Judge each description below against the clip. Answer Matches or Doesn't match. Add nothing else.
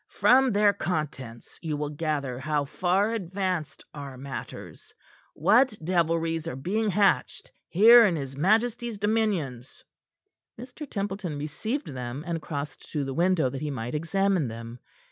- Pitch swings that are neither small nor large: Doesn't match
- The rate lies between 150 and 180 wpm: Doesn't match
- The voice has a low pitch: Doesn't match